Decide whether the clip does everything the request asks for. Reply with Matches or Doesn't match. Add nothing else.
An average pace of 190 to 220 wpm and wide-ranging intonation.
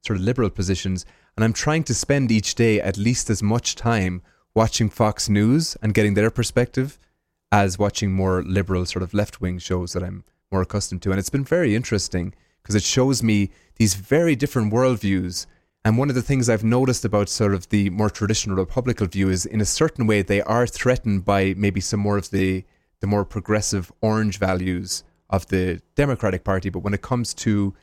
Doesn't match